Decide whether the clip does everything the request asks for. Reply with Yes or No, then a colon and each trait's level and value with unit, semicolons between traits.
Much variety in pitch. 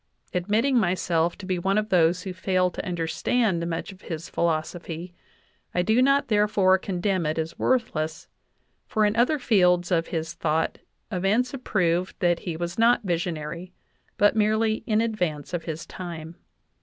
No: average, 4.1 semitones